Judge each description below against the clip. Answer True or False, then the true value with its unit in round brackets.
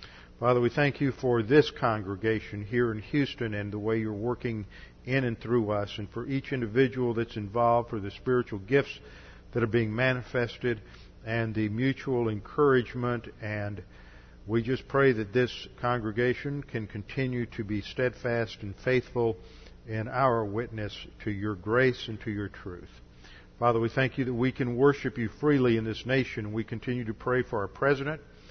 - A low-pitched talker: True (120 Hz)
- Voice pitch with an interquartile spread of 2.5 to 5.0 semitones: True (3.1 semitones)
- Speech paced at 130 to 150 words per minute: False (170 wpm)